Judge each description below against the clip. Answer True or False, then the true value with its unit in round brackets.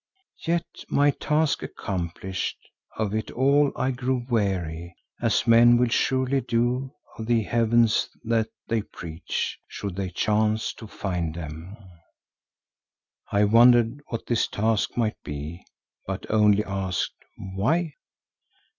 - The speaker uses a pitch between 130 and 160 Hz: False (110 Hz)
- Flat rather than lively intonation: False (4.1 semitones)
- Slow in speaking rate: True (120 wpm)